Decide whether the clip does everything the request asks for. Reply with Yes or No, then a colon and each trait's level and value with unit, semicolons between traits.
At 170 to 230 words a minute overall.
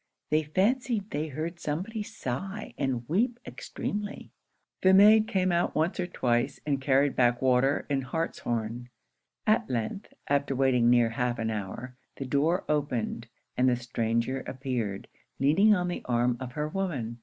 No: average, 155 wpm